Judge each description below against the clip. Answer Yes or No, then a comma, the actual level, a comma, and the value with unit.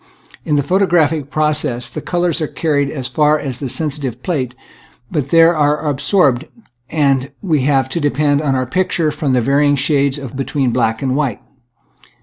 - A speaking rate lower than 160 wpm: No, average, 175 wpm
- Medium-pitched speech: Yes, medium, 145 Hz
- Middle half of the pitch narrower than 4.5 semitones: Yes, average, 2.7 semitones